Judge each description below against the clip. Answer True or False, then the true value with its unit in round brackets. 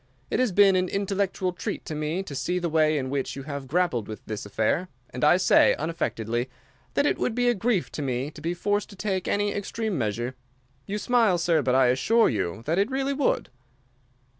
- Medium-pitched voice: True (175 Hz)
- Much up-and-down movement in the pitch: True (7.4 semitones)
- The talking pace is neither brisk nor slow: False (215 wpm)